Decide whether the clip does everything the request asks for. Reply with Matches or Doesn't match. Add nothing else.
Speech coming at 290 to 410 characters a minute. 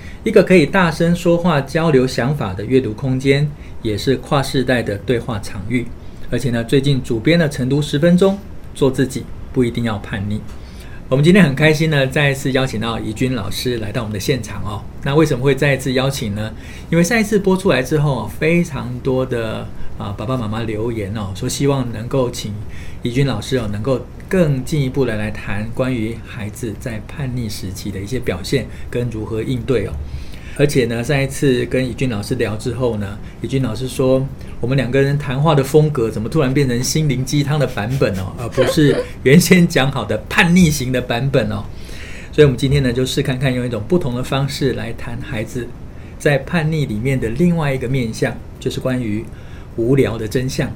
Matches